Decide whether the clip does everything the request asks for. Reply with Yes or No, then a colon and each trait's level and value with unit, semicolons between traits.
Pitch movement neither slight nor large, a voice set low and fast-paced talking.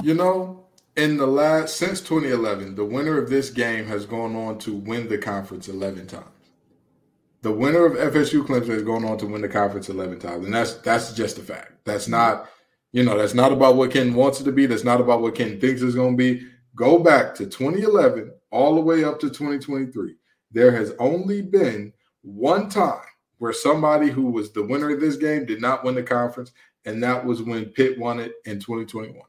Yes: average, 4.7 semitones; low, 125 Hz; fast, 220 wpm